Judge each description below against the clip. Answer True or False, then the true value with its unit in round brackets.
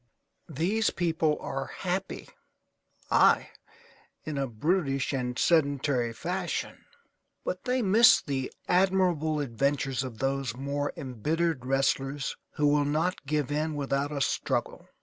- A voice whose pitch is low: False (145 Hz)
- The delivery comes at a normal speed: False (120 wpm)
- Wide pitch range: False (3.7 semitones)